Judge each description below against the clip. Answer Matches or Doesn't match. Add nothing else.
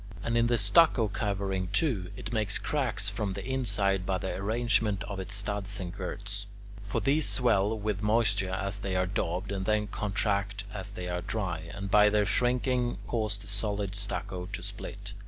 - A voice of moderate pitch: Doesn't match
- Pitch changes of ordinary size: Doesn't match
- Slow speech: Doesn't match